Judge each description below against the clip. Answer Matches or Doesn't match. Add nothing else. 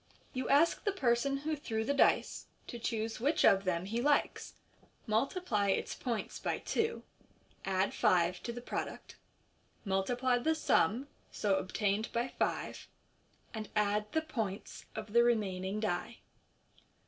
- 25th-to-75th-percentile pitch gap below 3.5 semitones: Doesn't match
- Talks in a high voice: Matches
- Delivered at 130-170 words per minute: Matches